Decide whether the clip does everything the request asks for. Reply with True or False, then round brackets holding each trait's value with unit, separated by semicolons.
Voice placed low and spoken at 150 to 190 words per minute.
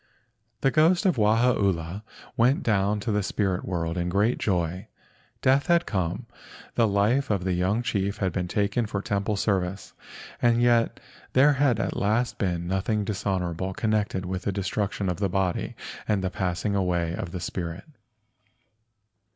True (100 Hz; 160 wpm)